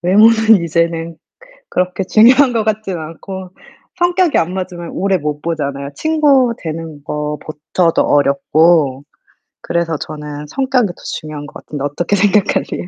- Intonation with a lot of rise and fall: Yes, wide, 5.9 semitones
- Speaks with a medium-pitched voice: Yes, medium, 170 Hz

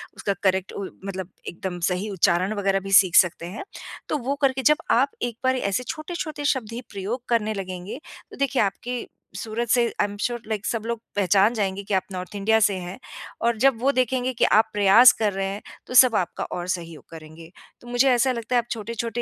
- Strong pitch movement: No, average, 4.2 semitones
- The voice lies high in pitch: Yes, high, 215 Hz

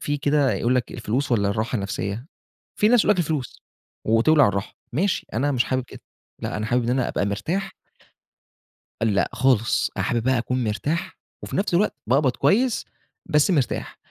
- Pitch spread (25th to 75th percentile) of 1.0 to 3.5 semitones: No, average, 5.1 semitones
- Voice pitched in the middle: No, low, 130 Hz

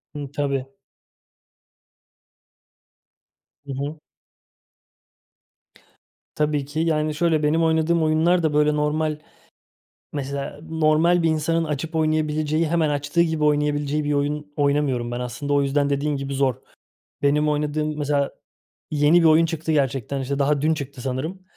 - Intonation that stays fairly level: Yes, narrow, 1.8 semitones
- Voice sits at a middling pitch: Yes, medium, 150 Hz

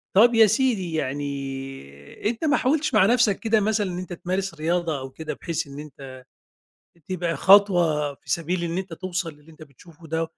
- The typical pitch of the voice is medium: Yes, medium, 170 Hz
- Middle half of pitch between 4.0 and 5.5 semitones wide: Yes, average, 5.0 semitones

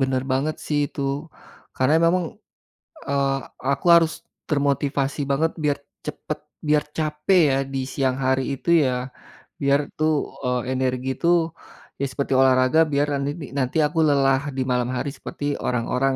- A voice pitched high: No, medium, 140 Hz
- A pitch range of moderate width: No, narrow, 2.3 semitones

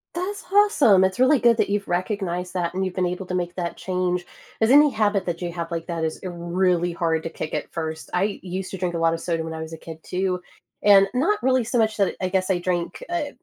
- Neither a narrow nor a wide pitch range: Yes, average, 3.3 semitones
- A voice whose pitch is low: No, medium, 185 Hz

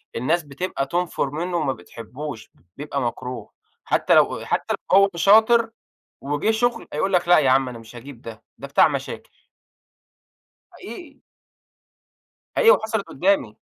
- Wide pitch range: Yes, wide, 7.2 semitones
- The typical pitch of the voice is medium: Yes, medium, 155 Hz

